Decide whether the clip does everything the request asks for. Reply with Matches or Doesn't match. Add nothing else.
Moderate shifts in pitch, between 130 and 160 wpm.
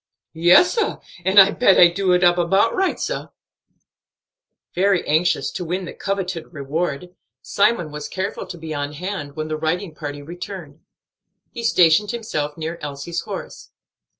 Matches